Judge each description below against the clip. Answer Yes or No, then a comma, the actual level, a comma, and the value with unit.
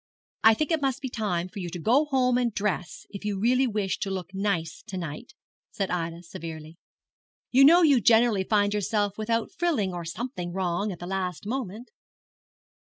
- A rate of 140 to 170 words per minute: No, average, 185 wpm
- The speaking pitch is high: Yes, high, 205 Hz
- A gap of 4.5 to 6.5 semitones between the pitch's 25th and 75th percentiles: Yes, average, 5.1 semitones